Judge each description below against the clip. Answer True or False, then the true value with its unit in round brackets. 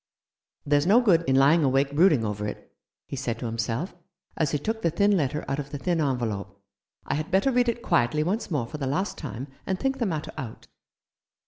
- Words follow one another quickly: True (220 wpm)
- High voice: False (150 Hz)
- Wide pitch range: True (6.3 semitones)